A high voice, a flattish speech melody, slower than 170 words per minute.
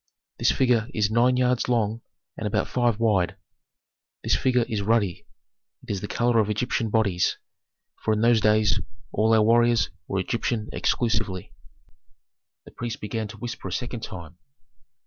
No: low, 110 Hz; narrow, 2.2 semitones; average, 155 wpm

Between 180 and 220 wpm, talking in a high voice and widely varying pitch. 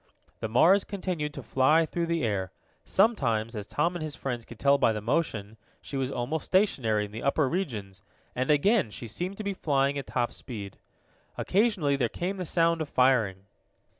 No: average, 190 wpm; medium, 140 Hz; wide, 6.9 semitones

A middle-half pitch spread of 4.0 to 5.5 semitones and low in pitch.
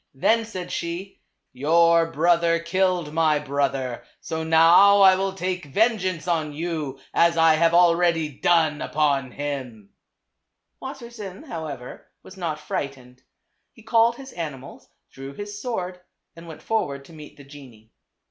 No: average, 4.3 semitones; medium, 165 Hz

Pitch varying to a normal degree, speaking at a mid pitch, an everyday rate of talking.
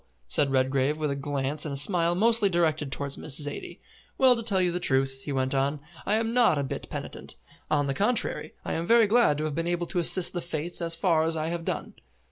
No: average, 4.1 semitones; medium, 160 Hz; fast, 240 wpm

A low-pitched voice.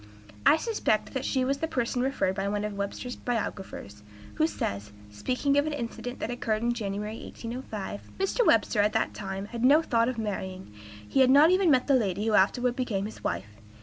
No: high, 230 Hz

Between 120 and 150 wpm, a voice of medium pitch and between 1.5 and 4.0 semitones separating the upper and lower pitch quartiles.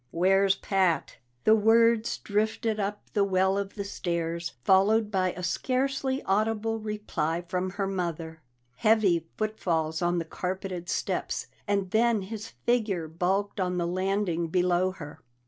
No: average, 140 wpm; high, 195 Hz; average, 3.4 semitones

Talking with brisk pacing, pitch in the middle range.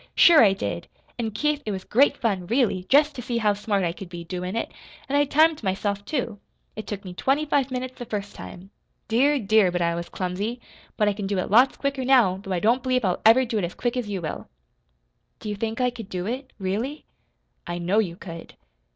No: fast, 230 wpm; high, 215 Hz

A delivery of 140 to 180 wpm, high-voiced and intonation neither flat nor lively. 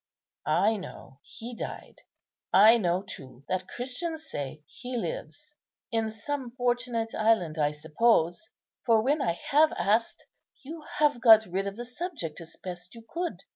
No: average, 150 wpm; high, 225 Hz; wide, 5.8 semitones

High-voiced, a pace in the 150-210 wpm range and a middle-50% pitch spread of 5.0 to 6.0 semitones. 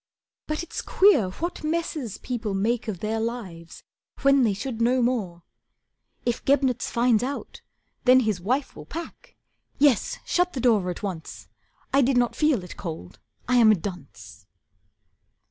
Yes: high, 235 Hz; average, 155 wpm; wide, 5.6 semitones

